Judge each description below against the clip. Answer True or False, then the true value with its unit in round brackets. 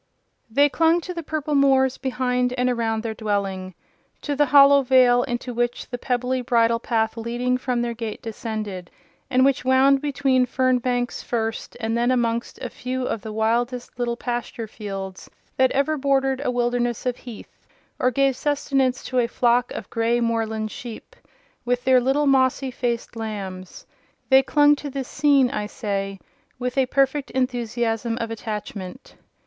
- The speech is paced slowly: False (160 wpm)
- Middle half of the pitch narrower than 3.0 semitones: True (2.6 semitones)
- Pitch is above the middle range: True (245 Hz)